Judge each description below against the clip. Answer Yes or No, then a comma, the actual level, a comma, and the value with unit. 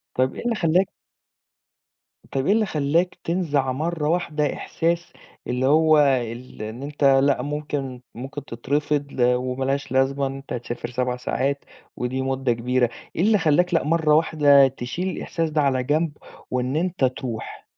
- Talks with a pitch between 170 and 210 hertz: No, medium, 140 Hz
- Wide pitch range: No, average, 3.7 semitones